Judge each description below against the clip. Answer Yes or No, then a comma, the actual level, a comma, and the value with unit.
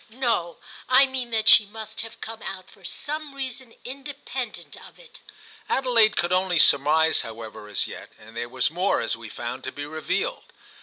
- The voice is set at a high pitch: Yes, high, 205 Hz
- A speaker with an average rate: Yes, average, 175 wpm